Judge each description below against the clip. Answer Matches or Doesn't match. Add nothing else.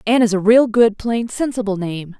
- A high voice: Matches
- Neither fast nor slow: Doesn't match